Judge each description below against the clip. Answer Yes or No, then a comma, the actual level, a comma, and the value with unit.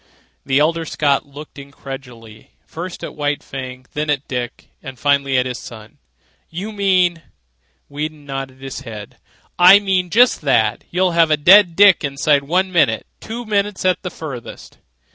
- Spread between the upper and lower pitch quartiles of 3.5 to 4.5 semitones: No, average, 5.3 semitones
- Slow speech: No, average, 160 wpm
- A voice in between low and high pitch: Yes, medium, 145 Hz